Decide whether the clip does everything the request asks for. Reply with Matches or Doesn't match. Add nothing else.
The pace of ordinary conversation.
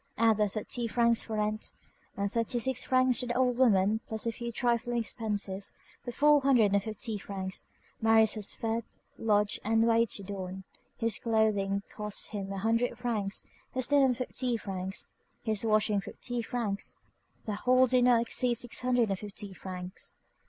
Matches